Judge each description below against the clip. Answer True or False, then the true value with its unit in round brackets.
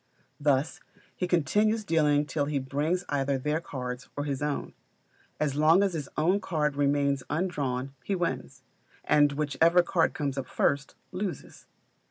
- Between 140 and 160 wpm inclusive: True (150 wpm)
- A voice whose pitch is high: False (150 Hz)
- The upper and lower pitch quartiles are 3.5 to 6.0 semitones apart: False (3.1 semitones)